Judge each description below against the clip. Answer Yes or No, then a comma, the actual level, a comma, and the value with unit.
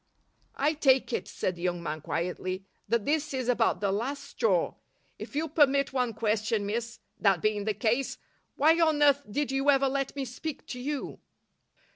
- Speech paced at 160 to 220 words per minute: Yes, average, 180 wpm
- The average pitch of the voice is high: Yes, very high, 250 Hz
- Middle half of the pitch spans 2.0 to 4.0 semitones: No, average, 5.2 semitones